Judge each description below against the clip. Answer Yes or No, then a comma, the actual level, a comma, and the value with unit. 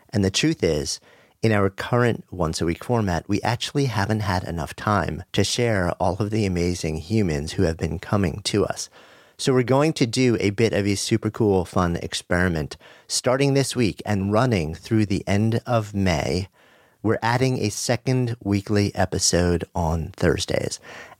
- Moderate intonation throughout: Yes, average, 4.5 semitones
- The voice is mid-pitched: No, low, 100 Hz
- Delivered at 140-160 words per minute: No, average, 175 wpm